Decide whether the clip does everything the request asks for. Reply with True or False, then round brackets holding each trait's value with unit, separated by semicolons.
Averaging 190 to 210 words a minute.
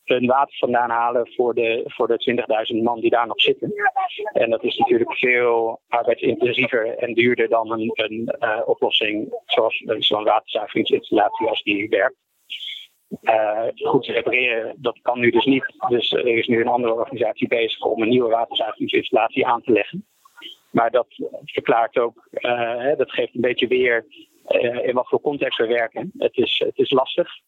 False (175 wpm)